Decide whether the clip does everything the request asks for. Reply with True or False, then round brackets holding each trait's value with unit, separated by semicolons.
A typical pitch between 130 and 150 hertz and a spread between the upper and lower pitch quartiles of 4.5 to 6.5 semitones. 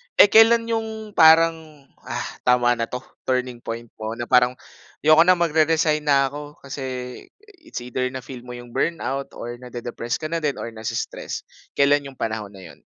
True (140 Hz; 4.8 semitones)